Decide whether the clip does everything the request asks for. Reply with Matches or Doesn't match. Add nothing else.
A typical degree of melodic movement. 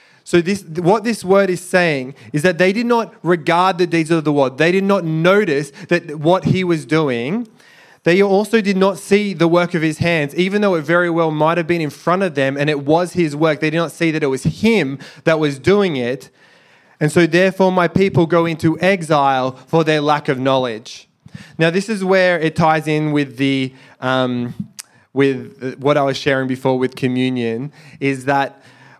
Matches